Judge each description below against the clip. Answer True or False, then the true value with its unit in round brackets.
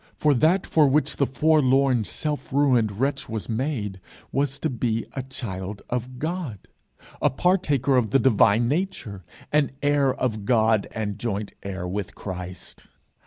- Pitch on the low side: True (125 Hz)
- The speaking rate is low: False (150 wpm)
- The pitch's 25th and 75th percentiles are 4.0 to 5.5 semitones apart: True (5.2 semitones)